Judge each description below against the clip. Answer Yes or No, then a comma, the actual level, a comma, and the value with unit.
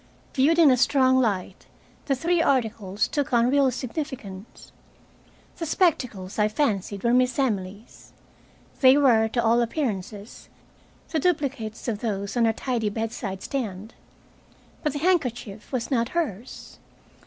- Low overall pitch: No, high, 240 Hz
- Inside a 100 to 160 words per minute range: Yes, slow, 135 wpm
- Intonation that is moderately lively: Yes, average, 4.6 semitones